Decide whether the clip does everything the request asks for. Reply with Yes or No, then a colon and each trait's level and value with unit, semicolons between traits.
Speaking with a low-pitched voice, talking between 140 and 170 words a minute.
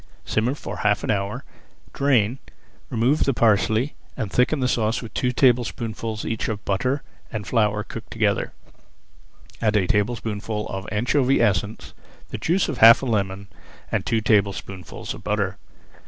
Yes: low, 110 Hz; average, 150 wpm